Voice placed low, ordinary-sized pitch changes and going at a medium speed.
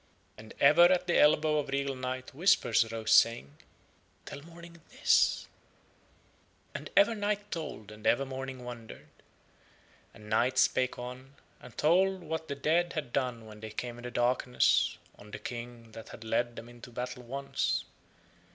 Yes: low, 130 Hz; average, 4.6 semitones; average, 160 wpm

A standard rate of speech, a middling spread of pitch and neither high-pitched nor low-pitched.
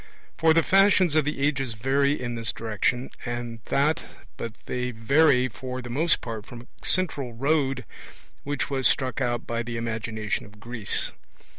No: average, 165 wpm; average, 3.5 semitones; low, 125 Hz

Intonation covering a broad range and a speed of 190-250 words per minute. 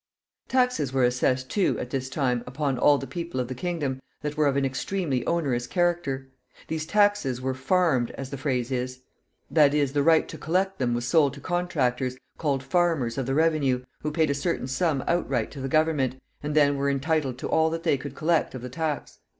No: average, 3.7 semitones; fast, 205 wpm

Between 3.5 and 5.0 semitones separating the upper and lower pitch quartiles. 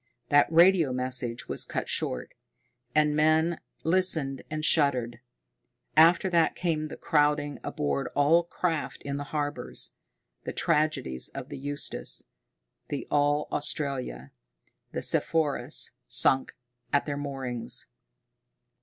No: average, 2.7 semitones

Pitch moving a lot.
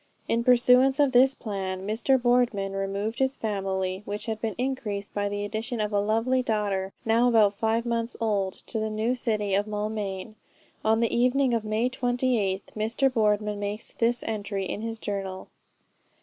No: average, 3.0 semitones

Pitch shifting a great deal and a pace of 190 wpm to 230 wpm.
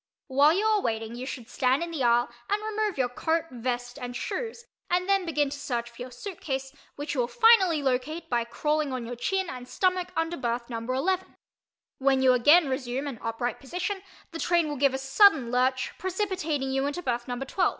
Yes: wide, 5.8 semitones; fast, 205 wpm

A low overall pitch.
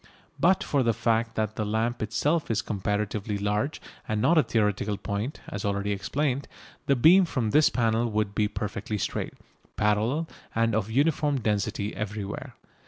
Yes: low, 110 Hz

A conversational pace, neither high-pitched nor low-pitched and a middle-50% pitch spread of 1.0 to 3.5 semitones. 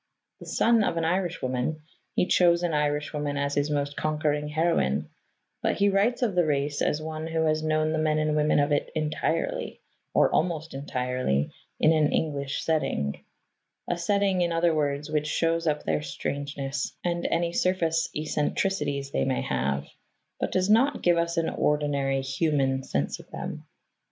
Yes: average, 165 wpm; medium, 155 Hz; average, 2.8 semitones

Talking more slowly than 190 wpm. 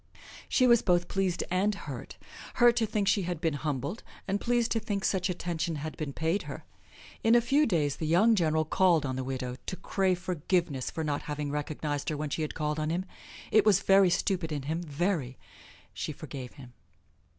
No: average, 200 wpm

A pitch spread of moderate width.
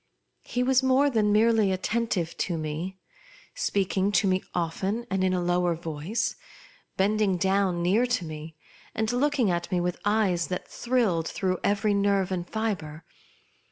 Yes: average, 3.8 semitones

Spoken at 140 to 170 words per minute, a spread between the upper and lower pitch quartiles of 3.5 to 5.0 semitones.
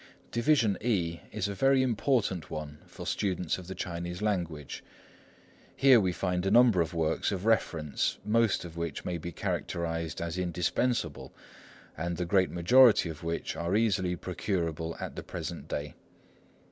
Yes: average, 155 wpm; average, 4.2 semitones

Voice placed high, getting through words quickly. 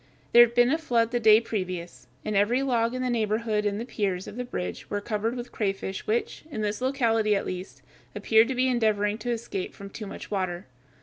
Yes: high, 220 Hz; fast, 220 wpm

